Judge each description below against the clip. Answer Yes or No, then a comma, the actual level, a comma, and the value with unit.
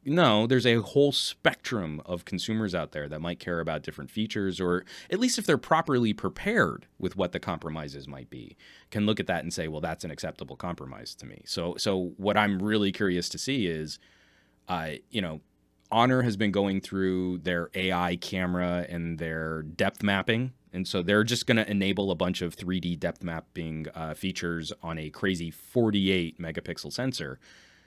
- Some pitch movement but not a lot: Yes, average, 4.0 semitones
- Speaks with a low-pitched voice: Yes, very low, 95 Hz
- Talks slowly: No, average, 185 wpm